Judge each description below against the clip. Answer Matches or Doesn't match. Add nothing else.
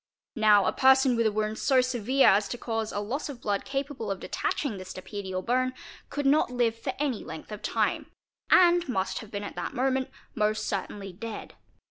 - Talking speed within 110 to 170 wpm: Doesn't match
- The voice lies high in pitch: Matches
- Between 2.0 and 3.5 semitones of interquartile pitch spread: Doesn't match